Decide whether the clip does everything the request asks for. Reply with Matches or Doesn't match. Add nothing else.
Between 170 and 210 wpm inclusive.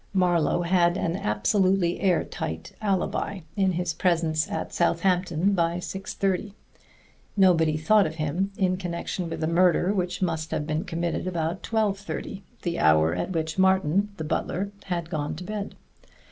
Doesn't match